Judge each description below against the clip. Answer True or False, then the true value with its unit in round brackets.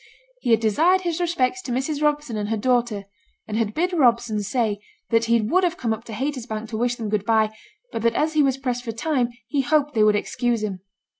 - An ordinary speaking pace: False (230 wpm)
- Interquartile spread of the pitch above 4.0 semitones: True (5.0 semitones)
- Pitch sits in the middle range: False (240 Hz)